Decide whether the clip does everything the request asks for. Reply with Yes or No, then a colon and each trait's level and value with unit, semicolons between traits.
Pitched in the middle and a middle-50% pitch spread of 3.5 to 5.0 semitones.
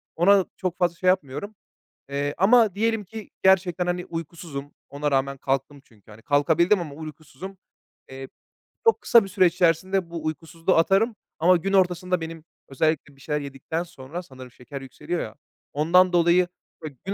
Yes: medium, 170 Hz; average, 4.4 semitones